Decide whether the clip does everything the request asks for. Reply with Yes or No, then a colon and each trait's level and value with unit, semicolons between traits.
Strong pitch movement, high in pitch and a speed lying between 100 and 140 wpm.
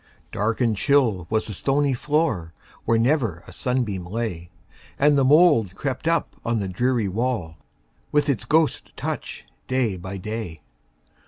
No: wide, 6.4 semitones; low, 115 Hz; slow, 135 wpm